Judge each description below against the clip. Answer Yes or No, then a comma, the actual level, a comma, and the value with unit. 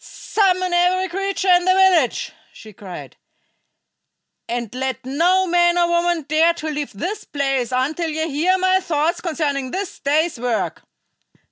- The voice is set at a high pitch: Yes, very high, 335 Hz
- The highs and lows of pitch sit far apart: No, average, 4.8 semitones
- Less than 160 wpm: Yes, average, 145 wpm